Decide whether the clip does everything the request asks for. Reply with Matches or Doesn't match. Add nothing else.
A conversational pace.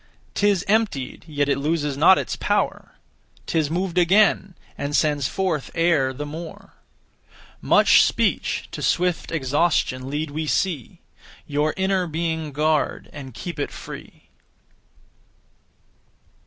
Doesn't match